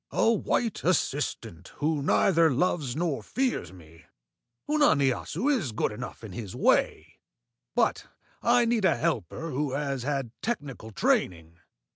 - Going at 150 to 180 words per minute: No, slow, 135 wpm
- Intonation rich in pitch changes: Yes, wide, 8.0 semitones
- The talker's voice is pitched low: No, medium, 145 Hz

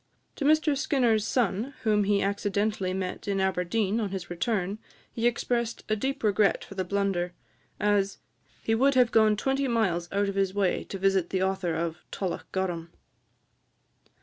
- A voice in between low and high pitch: No, high, 200 Hz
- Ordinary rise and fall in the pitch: Yes, average, 3.1 semitones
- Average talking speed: Yes, average, 160 wpm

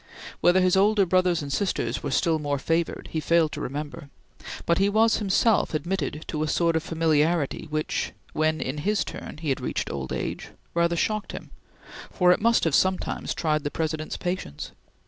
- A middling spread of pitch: Yes, average, 3.4 semitones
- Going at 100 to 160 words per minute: No, average, 185 wpm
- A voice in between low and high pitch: Yes, medium, 165 Hz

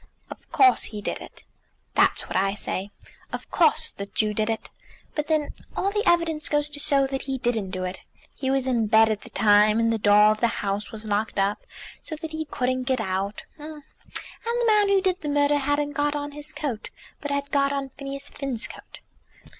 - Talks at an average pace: No, fast, 210 wpm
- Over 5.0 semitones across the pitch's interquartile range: Yes, wide, 5.6 semitones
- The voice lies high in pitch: Yes, very high, 270 Hz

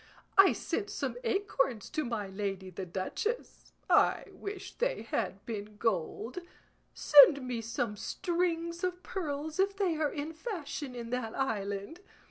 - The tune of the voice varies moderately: No, wide, 8.8 semitones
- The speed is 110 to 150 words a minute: Yes, average, 140 wpm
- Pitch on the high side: Yes, very high, 280 Hz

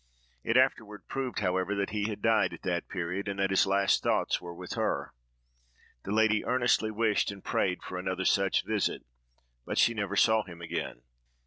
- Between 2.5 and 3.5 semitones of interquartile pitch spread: Yes, average, 2.8 semitones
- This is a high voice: No, low, 100 Hz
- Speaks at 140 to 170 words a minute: No, average, 185 wpm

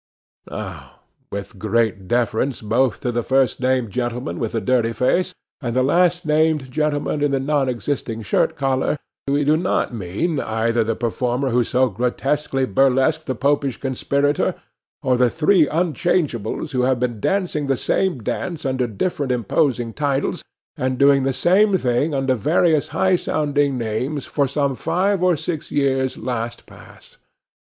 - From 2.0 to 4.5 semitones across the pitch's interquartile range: Yes, average, 3.7 semitones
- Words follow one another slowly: No, average, 155 wpm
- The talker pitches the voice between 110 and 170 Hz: Yes, low, 135 Hz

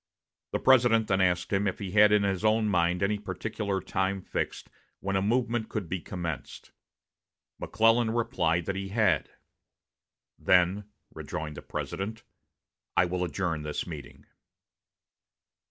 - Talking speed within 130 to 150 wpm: Yes, average, 140 wpm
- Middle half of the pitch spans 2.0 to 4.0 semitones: Yes, average, 3.3 semitones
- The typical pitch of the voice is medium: No, very low, 95 Hz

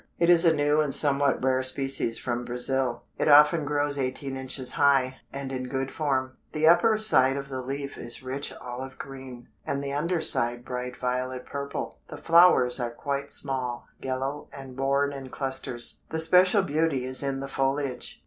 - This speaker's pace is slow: No, average, 175 wpm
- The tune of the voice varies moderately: No, narrow, 2.0 semitones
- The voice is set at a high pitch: No, low, 135 Hz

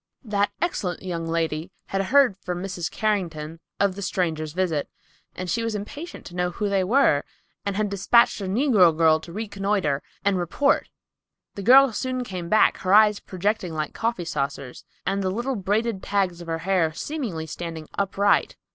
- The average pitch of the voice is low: No, high, 190 Hz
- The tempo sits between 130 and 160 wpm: No, average, 175 wpm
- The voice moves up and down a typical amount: Yes, average, 4.0 semitones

